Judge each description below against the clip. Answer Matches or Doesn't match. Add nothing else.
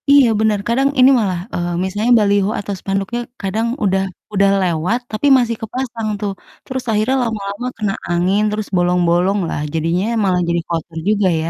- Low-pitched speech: Doesn't match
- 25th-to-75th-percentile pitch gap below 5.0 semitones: Matches